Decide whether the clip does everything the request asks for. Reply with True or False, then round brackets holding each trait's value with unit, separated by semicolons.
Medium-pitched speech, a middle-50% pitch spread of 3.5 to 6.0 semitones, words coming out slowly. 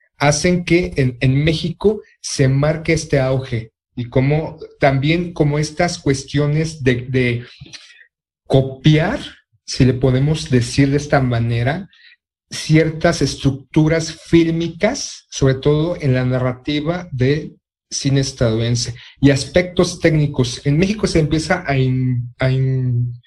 True (145 Hz; 3.9 semitones; 120 wpm)